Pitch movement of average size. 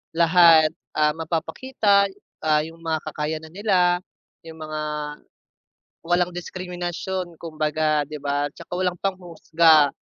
No: narrow, 2.3 semitones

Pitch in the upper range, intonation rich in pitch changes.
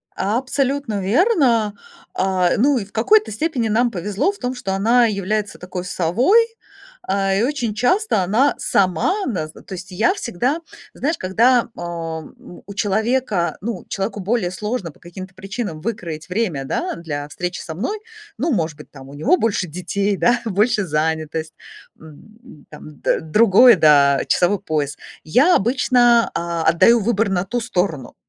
Yes: high, 200 Hz; wide, 5.7 semitones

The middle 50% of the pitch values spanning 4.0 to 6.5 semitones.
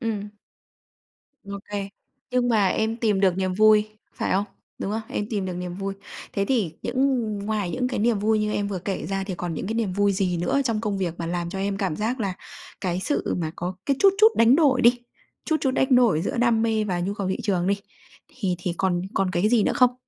No: average, 3.4 semitones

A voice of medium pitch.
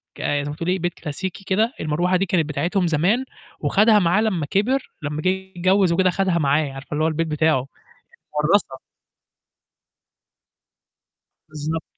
Yes: medium, 175 Hz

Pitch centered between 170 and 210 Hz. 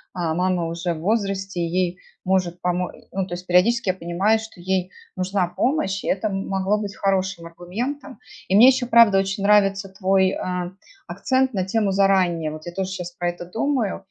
Yes: high, 190 Hz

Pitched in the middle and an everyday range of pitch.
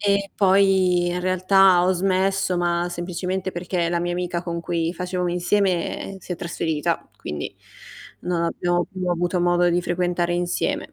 No: medium, 175 Hz; narrow, 1.2 semitones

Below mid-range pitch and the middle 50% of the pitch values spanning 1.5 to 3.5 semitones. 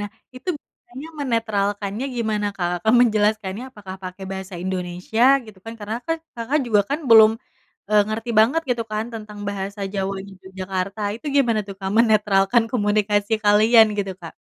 No: high, 210 Hz; narrow, 2.6 semitones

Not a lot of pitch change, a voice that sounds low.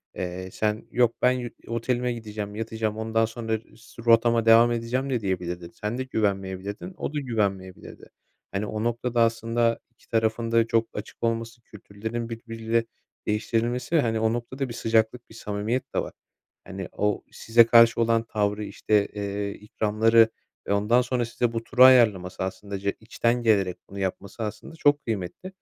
Yes: narrow, 2.2 semitones; low, 115 Hz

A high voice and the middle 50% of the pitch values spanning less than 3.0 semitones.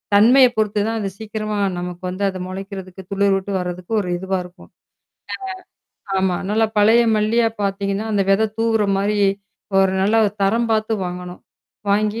Yes: high, 200 Hz; narrow, 2.4 semitones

